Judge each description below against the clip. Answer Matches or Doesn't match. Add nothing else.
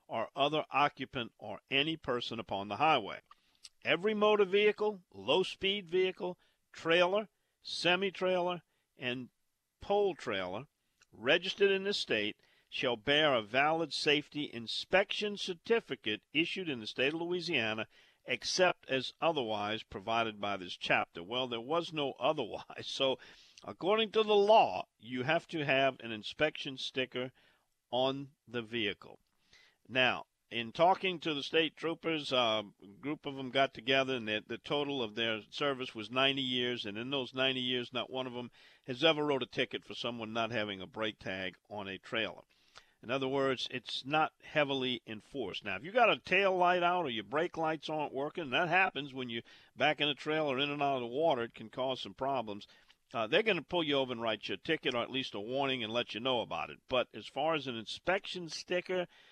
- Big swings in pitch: Matches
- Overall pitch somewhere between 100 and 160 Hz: Matches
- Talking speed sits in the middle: Matches